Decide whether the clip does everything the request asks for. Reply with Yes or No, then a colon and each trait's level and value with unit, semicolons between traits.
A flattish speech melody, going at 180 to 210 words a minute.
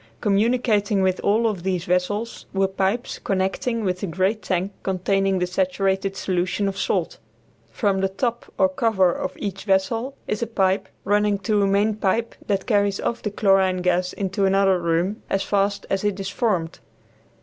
No: narrow, 1.8 semitones; average, 170 wpm